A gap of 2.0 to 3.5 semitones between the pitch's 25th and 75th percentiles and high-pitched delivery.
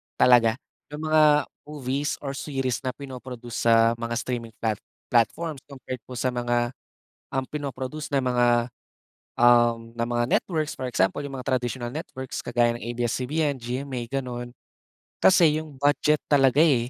No: average, 2.9 semitones; low, 130 Hz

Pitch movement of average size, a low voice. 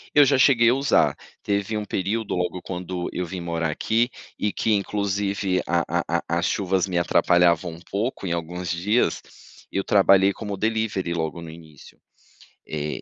Yes: average, 3.3 semitones; very low, 95 Hz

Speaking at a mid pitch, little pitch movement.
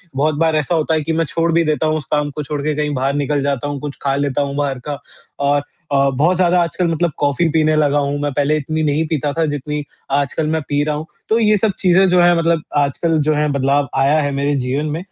Yes: medium, 150 Hz; narrow, 2.1 semitones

